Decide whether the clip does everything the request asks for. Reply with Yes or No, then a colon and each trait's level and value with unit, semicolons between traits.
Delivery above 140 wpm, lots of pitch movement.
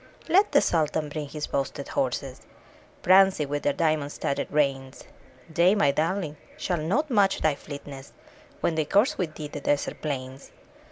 No: average, 160 wpm; average, 4.0 semitones